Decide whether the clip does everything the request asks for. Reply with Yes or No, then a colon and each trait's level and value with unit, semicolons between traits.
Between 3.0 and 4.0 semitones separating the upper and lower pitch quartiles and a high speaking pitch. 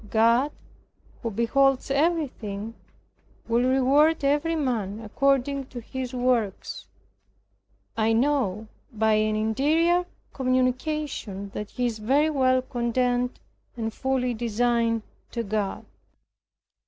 Yes: average, 3.7 semitones; high, 245 Hz